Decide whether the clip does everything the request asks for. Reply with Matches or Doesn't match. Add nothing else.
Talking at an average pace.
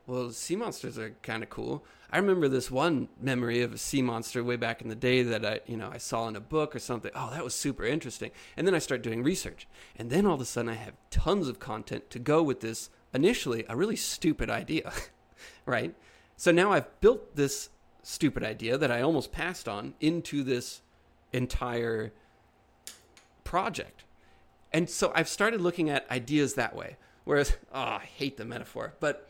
Matches